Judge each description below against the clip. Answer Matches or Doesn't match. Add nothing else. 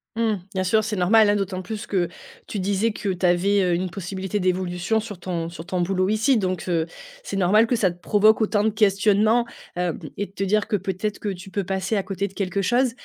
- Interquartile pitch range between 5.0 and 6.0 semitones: Doesn't match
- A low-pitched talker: Doesn't match